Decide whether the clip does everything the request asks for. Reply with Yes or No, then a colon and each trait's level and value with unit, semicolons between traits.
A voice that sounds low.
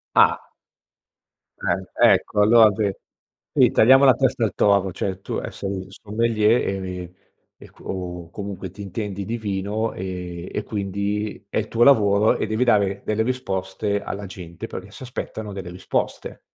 Yes: low, 100 Hz